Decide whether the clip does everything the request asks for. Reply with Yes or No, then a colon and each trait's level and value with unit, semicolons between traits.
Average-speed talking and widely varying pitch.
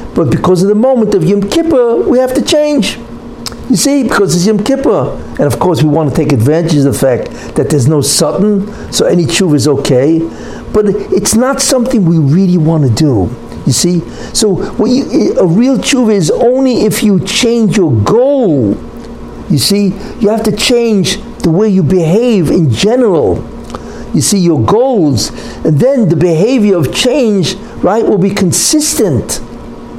Yes: average, 170 wpm; wide, 6.0 semitones